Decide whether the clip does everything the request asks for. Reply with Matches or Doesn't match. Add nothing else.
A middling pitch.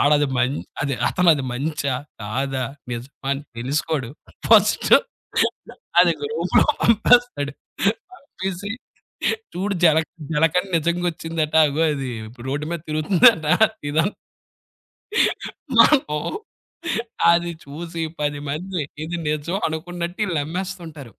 Matches